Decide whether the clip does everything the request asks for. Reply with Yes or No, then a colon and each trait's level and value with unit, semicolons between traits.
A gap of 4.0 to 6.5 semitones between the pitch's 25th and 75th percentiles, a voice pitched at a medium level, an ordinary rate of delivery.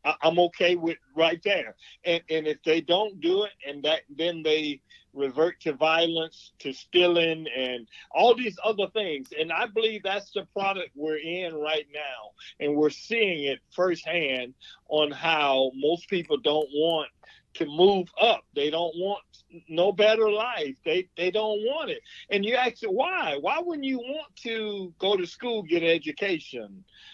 Yes: average, 5.3 semitones; medium, 170 Hz; average, 170 wpm